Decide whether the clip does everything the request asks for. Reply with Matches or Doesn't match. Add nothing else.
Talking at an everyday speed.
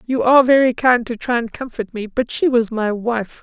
Doesn't match